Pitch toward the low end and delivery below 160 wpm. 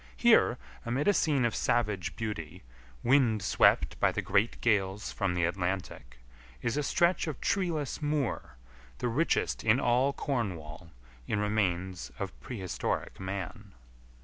Yes: low, 105 Hz; slow, 135 wpm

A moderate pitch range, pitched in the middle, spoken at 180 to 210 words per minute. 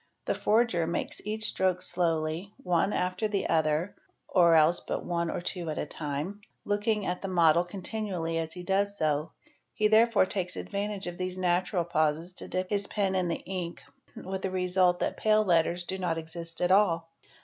Yes: average, 3.0 semitones; medium, 180 Hz; average, 190 wpm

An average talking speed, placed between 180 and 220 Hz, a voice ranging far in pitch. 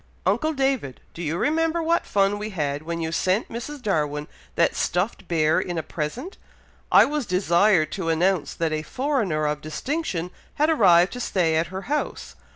Yes: average, 175 wpm; medium, 185 Hz; wide, 8.1 semitones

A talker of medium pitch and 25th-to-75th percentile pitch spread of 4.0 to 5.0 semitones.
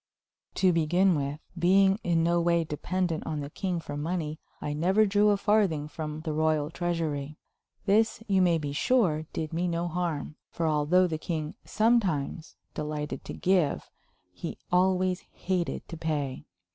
No: medium, 170 Hz; average, 3.3 semitones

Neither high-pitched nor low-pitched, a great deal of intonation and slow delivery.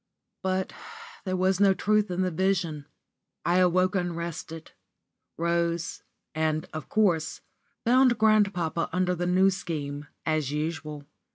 No: medium, 175 Hz; average, 3.0 semitones; slow, 125 wpm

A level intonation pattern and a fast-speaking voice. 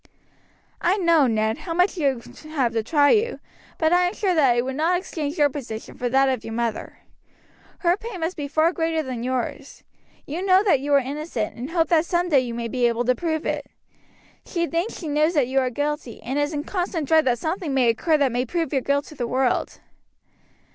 No: average, 4.9 semitones; fast, 225 wpm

